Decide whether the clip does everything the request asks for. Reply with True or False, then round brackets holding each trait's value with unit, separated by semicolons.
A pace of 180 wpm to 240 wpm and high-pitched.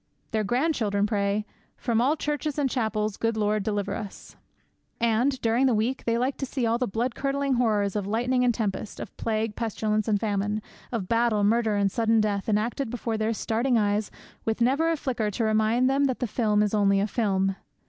True (200 wpm; 225 Hz)